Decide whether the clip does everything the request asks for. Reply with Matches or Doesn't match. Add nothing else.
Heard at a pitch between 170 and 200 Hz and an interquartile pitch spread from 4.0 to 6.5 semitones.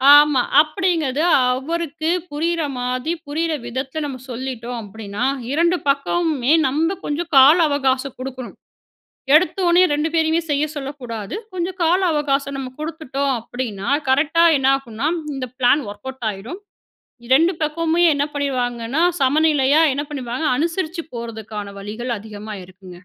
Doesn't match